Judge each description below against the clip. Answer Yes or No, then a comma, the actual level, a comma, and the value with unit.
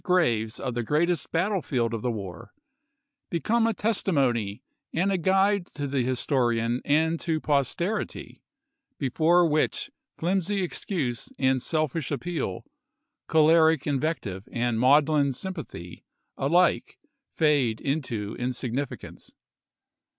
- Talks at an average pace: No, slow, 115 wpm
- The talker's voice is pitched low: No, medium, 145 Hz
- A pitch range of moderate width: No, wide, 5.8 semitones